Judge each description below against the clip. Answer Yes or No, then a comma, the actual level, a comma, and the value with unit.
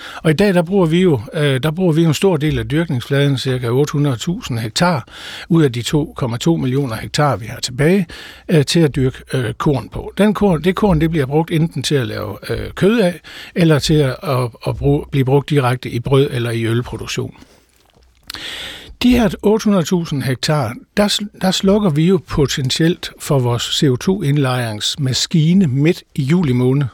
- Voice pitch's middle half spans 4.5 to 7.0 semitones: Yes, wide, 5.4 semitones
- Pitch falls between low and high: Yes, medium, 145 Hz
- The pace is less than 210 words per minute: Yes, average, 165 wpm